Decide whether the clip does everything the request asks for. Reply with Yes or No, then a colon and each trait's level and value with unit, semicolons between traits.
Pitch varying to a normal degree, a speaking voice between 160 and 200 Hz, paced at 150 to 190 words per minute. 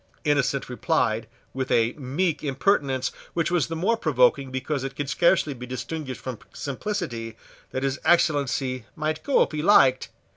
No: average, 3.6 semitones; medium, 140 Hz; average, 155 wpm